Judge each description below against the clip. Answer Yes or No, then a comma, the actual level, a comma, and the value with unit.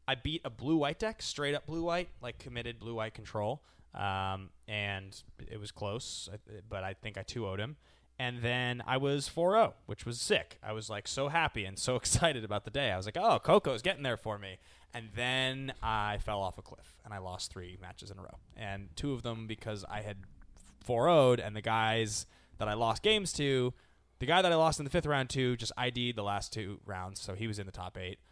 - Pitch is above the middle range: No, low, 110 Hz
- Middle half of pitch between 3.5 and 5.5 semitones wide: Yes, average, 4.5 semitones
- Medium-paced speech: No, fast, 230 wpm